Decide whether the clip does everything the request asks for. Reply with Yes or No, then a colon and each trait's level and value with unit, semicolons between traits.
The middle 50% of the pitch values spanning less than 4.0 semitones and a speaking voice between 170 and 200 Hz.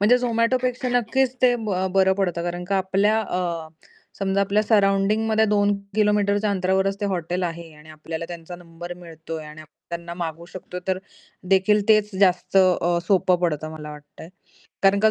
Yes: average, 3.5 semitones; high, 190 Hz